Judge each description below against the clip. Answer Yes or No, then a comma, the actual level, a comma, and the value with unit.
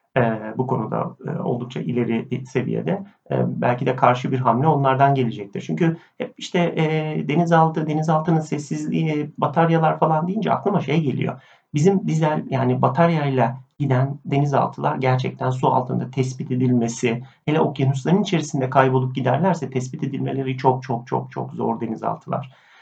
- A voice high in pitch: No, low, 135 Hz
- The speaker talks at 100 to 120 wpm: No, average, 135 wpm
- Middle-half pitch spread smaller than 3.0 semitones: No, average, 3.8 semitones